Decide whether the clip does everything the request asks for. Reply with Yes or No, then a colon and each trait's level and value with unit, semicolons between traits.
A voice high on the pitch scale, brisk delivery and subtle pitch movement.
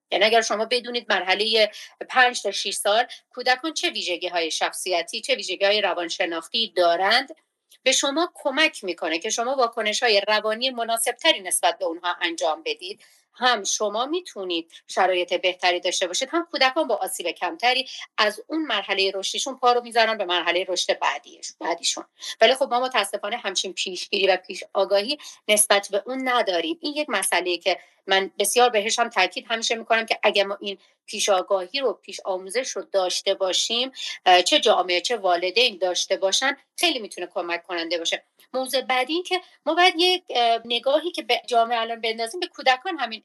No: high, 215 Hz; fast, 165 wpm; average, 5.2 semitones